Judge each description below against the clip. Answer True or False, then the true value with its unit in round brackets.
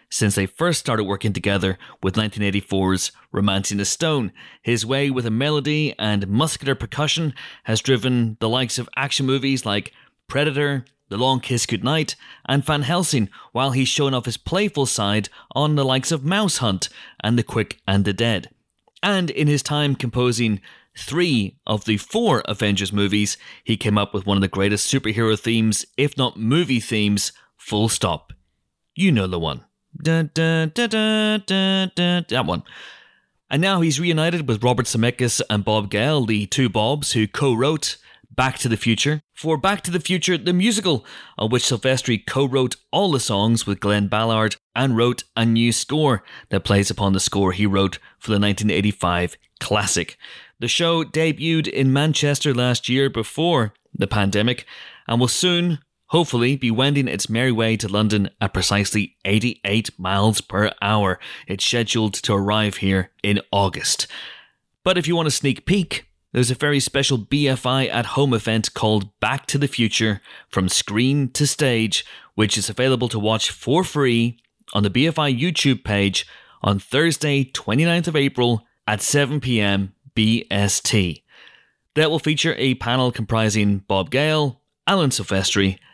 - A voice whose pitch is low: True (120 Hz)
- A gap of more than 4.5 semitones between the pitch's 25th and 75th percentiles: True (5.5 semitones)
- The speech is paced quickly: False (165 wpm)